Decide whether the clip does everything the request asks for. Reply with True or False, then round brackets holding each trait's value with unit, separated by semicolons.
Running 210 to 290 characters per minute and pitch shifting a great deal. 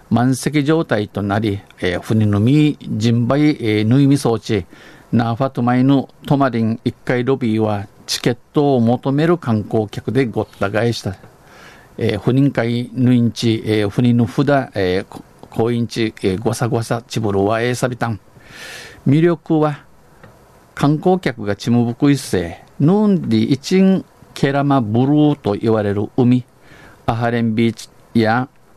False (270 characters per minute; 3.8 semitones)